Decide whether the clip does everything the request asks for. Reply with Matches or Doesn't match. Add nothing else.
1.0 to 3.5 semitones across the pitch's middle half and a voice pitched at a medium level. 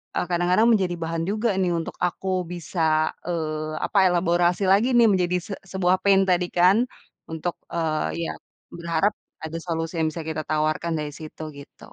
Matches